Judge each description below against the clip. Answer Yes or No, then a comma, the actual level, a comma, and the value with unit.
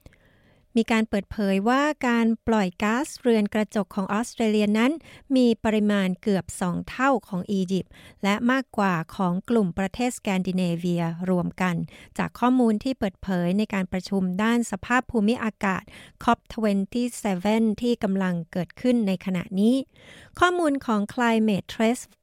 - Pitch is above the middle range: Yes, high, 215 Hz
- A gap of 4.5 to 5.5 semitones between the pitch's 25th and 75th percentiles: No, average, 3.8 semitones